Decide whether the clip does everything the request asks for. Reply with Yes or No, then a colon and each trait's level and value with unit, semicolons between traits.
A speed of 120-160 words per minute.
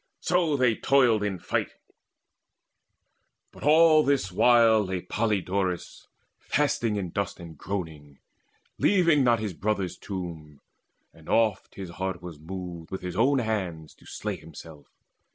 Yes: slow, 135 wpm